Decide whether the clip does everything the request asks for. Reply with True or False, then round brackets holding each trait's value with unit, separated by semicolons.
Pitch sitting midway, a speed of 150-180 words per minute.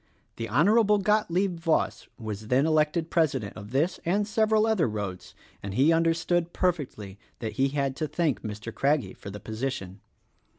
True (145 Hz; 160 wpm)